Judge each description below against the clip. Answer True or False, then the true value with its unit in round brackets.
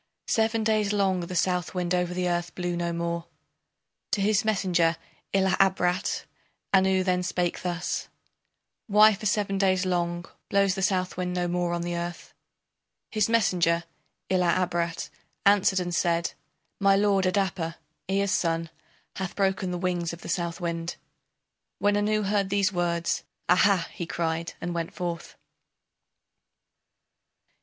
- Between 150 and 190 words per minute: False (135 wpm)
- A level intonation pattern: True (2.3 semitones)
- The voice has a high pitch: False (180 Hz)